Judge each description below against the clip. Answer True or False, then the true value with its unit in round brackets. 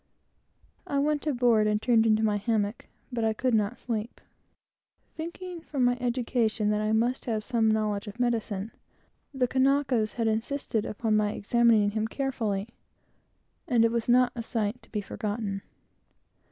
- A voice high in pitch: True (225 Hz)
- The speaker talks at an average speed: True (155 wpm)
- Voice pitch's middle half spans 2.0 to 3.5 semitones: True (2.6 semitones)